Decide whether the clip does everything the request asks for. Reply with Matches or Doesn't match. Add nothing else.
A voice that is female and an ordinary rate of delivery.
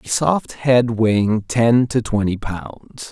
Doesn't match